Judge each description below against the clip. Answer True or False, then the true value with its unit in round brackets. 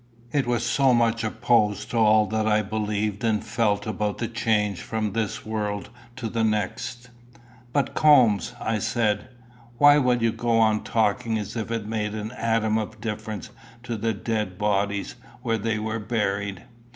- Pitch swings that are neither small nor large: False (1.7 semitones)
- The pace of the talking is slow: False (165 wpm)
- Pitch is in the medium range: False (110 Hz)